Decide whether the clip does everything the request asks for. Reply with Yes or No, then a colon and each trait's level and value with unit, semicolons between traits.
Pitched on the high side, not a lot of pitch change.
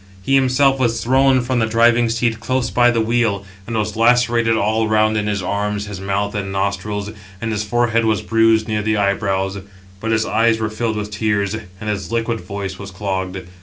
No: low, 110 Hz; narrow, 2.3 semitones